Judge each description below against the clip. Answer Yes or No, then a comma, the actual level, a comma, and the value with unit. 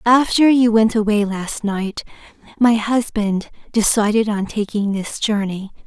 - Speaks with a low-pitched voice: No, high, 215 Hz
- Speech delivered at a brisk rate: No, slow, 135 wpm